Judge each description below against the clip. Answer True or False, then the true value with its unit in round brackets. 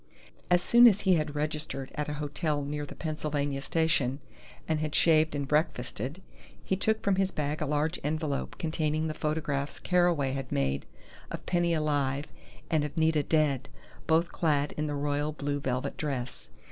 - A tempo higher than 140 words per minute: True (170 wpm)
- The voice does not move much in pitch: True (2.0 semitones)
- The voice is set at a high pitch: False (150 Hz)